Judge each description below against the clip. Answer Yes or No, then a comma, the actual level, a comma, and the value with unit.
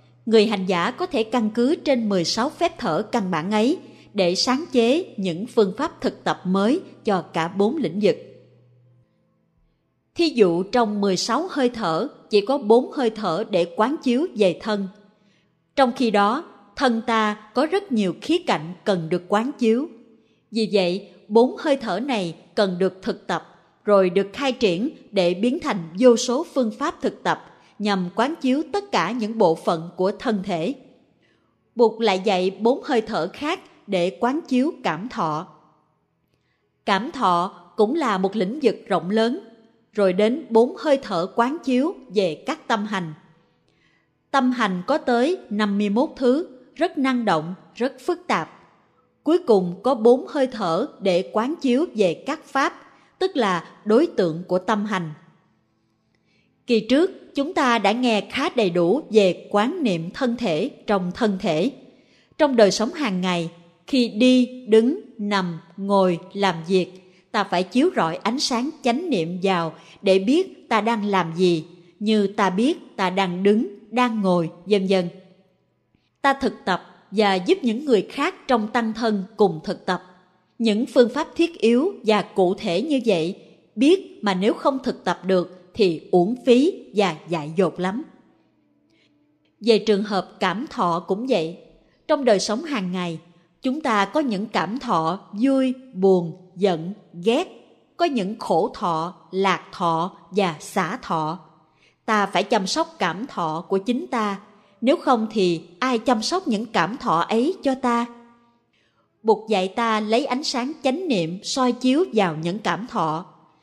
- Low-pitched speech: No, high, 215 Hz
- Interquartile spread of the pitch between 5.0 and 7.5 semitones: Yes, wide, 5.6 semitones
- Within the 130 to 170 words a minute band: Yes, slow, 165 wpm